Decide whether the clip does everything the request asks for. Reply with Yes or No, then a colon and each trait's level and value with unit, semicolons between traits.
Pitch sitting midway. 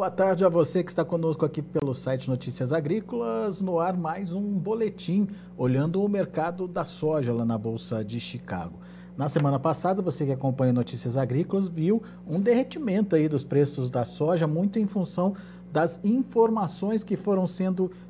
Yes: medium, 175 Hz